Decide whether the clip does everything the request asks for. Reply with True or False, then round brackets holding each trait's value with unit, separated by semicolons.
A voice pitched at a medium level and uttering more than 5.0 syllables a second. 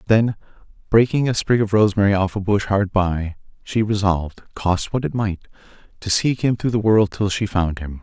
False (100 Hz; 5.2 syllables/s)